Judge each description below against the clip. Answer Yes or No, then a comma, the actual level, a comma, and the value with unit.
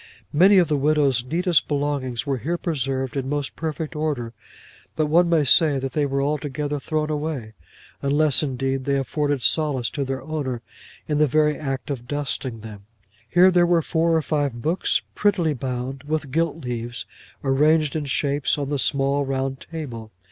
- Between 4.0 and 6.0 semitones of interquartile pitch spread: No, average, 2.7 semitones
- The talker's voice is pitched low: No, medium, 145 Hz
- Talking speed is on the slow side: No, average, 170 wpm